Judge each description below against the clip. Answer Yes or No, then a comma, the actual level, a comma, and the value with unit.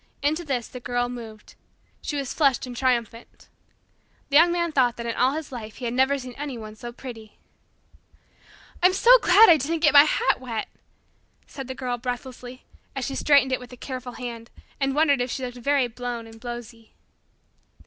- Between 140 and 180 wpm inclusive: No, average, 190 wpm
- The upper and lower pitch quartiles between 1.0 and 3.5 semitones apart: Yes, average, 2.8 semitones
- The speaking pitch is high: Yes, very high, 255 Hz